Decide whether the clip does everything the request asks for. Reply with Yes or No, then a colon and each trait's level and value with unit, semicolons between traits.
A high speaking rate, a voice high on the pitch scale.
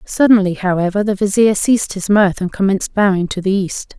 No: average, 195 wpm; high, 195 Hz